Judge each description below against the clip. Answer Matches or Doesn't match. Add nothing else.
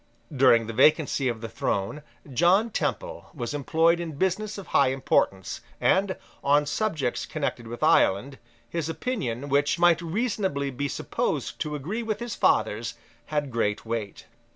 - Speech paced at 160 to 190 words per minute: Doesn't match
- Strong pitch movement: Matches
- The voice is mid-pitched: Matches